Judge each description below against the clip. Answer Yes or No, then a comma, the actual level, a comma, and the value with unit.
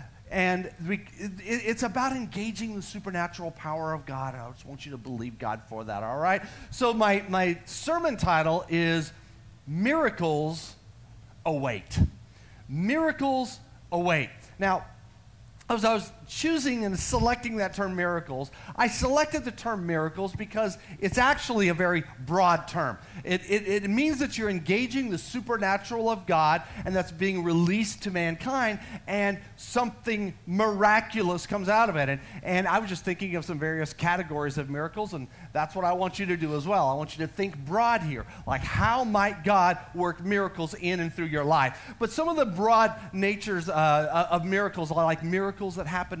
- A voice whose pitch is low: No, medium, 180 Hz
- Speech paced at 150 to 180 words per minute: Yes, average, 170 wpm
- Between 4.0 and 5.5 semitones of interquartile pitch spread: Yes, average, 5.1 semitones